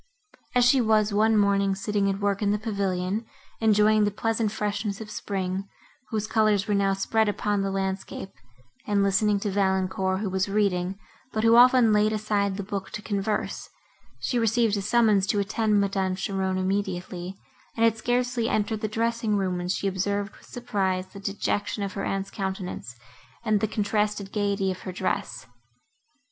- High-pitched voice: Yes, high, 205 Hz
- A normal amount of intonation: No, narrow, 1.8 semitones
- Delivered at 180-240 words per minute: No, average, 170 wpm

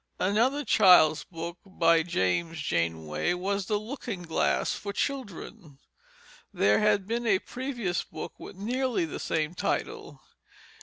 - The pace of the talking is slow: Yes, slow, 130 wpm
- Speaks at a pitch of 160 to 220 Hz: Yes, medium, 185 Hz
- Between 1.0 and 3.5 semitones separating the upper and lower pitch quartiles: No, average, 5.1 semitones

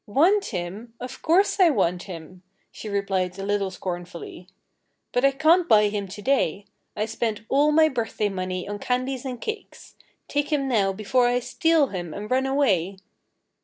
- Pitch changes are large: Yes, wide, 6.0 semitones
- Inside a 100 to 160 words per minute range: No, average, 170 wpm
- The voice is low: No, high, 215 Hz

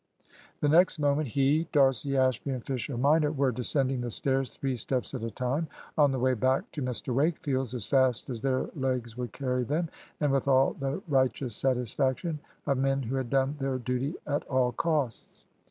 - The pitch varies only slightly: Yes, narrow, 2.0 semitones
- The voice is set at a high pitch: No, low, 135 Hz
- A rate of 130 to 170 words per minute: No, average, 185 wpm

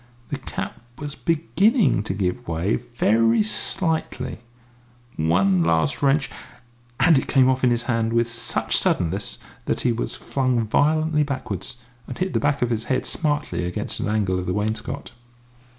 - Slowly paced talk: No, average, 160 wpm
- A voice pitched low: Yes, low, 120 Hz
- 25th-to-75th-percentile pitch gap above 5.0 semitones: Yes, wide, 5.5 semitones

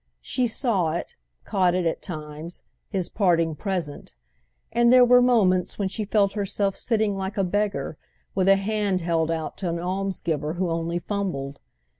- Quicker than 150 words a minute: Yes, average, 160 wpm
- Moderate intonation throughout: Yes, average, 3.5 semitones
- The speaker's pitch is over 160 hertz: Yes, high, 190 Hz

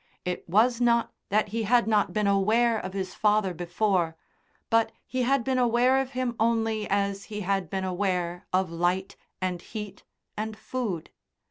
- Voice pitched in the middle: No, high, 210 Hz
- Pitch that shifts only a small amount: No, average, 3.7 semitones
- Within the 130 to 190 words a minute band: Yes, average, 165 wpm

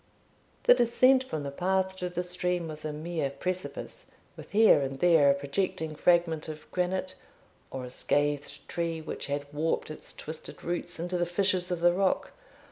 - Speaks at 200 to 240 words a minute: No, average, 175 wpm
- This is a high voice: No, medium, 170 Hz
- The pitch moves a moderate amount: Yes, average, 3.3 semitones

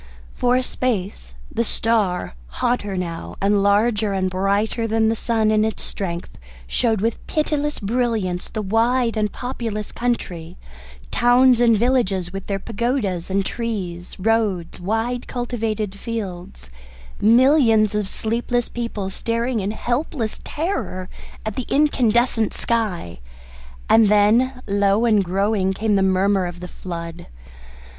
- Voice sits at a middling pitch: No, high, 215 Hz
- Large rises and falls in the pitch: No, average, 3.7 semitones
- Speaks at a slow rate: Yes, slow, 130 wpm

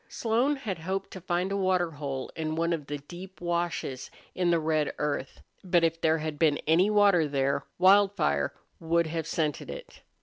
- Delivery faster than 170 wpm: Yes, average, 180 wpm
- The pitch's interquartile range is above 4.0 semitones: No, average, 3.5 semitones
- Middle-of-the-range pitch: Yes, medium, 170 Hz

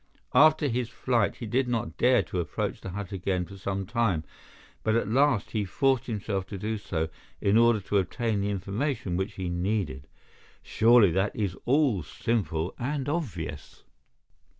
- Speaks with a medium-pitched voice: No, low, 105 Hz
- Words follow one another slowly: No, average, 165 wpm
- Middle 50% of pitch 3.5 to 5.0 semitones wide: Yes, average, 4.2 semitones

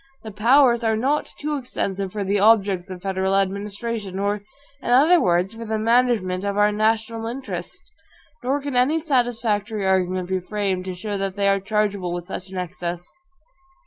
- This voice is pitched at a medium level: No, high, 205 Hz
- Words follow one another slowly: No, average, 175 wpm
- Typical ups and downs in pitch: Yes, average, 3.4 semitones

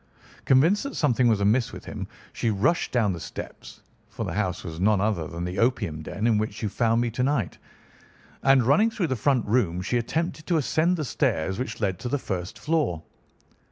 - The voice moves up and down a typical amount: No, wide, 6.0 semitones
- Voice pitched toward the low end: Yes, low, 115 Hz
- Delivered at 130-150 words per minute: No, average, 195 wpm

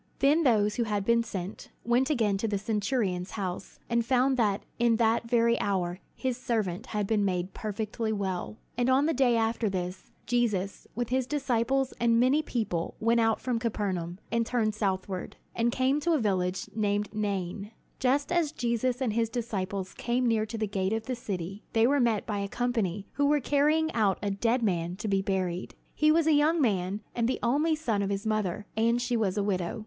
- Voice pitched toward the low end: No, high, 225 Hz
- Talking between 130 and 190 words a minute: No, average, 200 wpm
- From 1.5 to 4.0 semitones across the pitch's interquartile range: Yes, average, 3.7 semitones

